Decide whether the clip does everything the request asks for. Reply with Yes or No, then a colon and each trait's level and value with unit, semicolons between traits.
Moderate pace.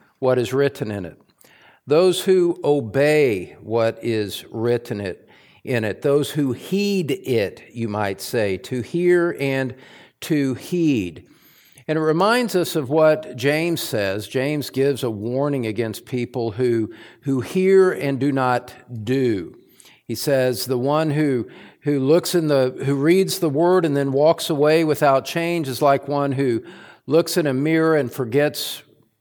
Yes: average, 155 wpm